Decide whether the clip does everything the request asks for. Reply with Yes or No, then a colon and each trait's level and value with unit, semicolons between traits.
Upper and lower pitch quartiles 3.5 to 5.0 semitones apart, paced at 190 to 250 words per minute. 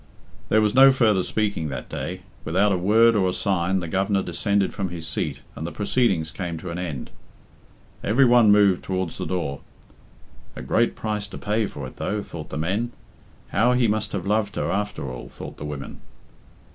Yes: average, 3.9 semitones; average, 195 wpm